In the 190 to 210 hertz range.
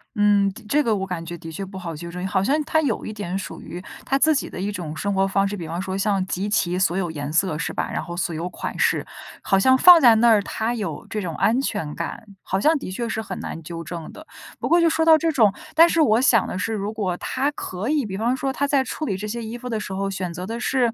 Yes: high, 205 Hz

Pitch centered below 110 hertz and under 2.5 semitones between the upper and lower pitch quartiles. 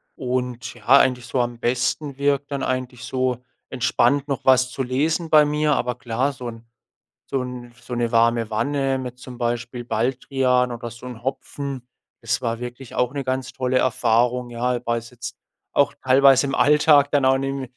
No: low, 125 Hz; narrow, 2.0 semitones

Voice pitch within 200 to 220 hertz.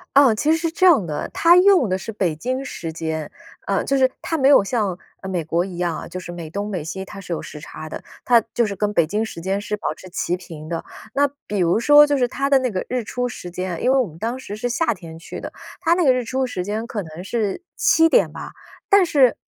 Yes: high, 210 Hz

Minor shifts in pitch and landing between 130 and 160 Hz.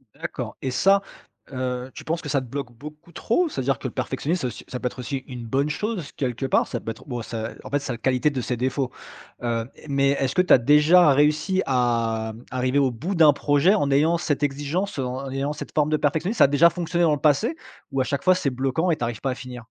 No: average, 3.5 semitones; medium, 140 Hz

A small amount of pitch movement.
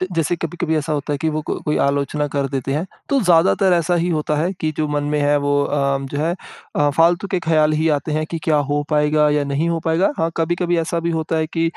Yes: narrow, 2.1 semitones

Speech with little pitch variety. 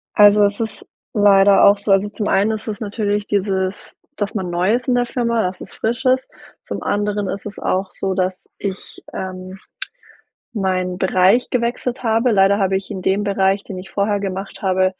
Yes: narrow, 2.0 semitones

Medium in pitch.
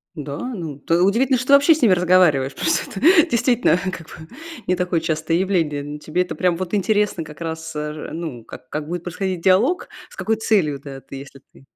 Yes: medium, 175 Hz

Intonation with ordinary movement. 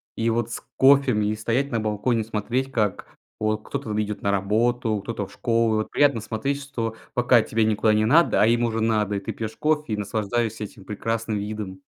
No: narrow, 2.1 semitones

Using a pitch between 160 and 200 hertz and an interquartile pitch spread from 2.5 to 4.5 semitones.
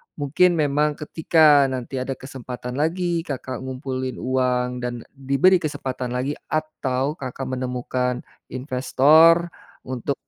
No: low, 130 Hz; average, 3.0 semitones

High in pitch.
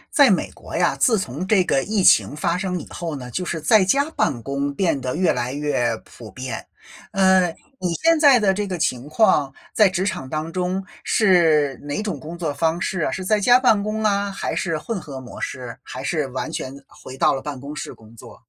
No: medium, 170 Hz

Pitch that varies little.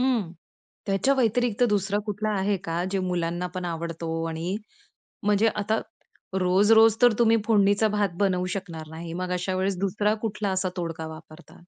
No: average, 3.3 semitones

